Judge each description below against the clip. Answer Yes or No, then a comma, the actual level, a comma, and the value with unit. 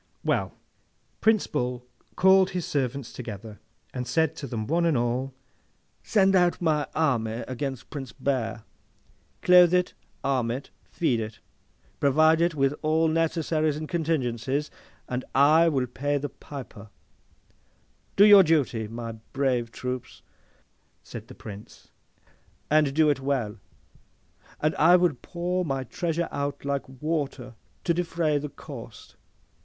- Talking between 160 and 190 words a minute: No, slow, 135 wpm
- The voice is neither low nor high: Yes, medium, 145 Hz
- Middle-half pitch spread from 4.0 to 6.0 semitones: Yes, average, 4.5 semitones